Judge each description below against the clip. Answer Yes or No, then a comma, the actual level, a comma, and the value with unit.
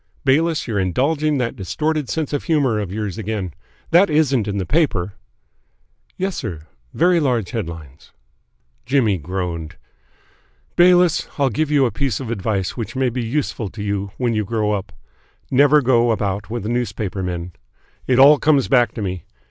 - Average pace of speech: Yes, average, 165 wpm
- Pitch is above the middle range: No, low, 115 Hz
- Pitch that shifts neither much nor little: No, wide, 6.3 semitones